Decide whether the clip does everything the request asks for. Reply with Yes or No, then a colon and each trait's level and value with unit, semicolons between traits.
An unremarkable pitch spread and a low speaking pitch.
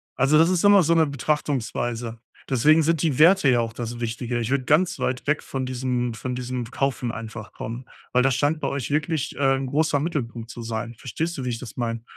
Yes: average, 4.2 semitones; low, 130 Hz